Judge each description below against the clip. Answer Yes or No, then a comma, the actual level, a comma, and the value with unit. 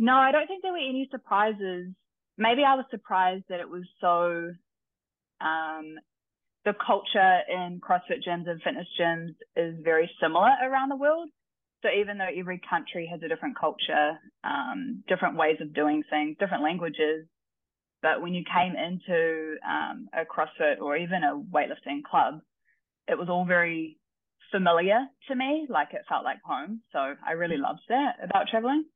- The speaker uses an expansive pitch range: Yes, wide, 6.9 semitones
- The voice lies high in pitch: No, medium, 180 Hz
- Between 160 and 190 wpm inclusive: Yes, average, 165 wpm